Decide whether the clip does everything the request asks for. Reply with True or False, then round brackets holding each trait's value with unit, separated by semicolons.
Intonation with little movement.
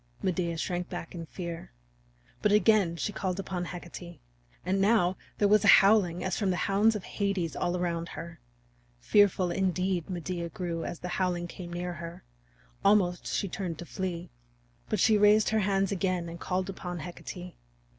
True (2.2 semitones)